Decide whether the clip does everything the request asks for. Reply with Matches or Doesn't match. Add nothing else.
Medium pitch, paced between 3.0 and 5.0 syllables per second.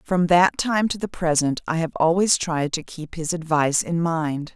Matches